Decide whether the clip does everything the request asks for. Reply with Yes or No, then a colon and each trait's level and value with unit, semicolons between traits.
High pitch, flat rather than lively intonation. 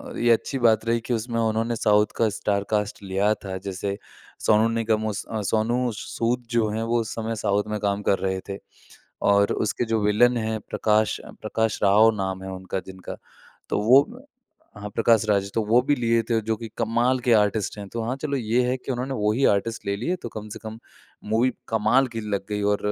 No: low, 110 Hz; narrow, 2.2 semitones